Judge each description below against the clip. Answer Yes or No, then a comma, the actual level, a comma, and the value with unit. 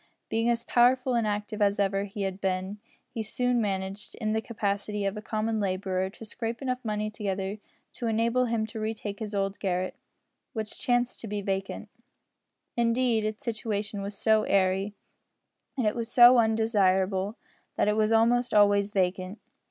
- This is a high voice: Yes, high, 210 Hz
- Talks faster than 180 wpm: No, average, 170 wpm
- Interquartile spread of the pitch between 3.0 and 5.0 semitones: No, narrow, 2.4 semitones